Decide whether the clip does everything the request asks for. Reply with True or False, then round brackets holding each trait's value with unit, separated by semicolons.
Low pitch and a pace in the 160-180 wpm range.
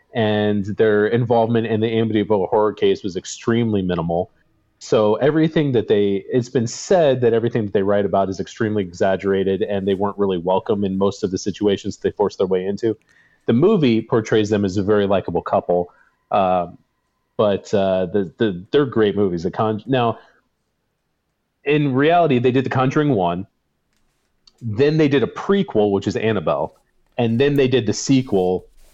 True (105 Hz; 170 wpm)